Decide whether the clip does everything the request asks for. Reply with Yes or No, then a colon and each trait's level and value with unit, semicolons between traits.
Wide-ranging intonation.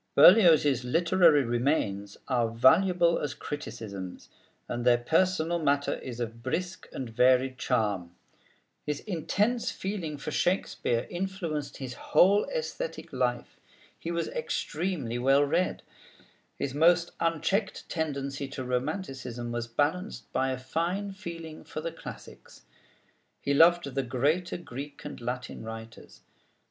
Yes: wide, 5.7 semitones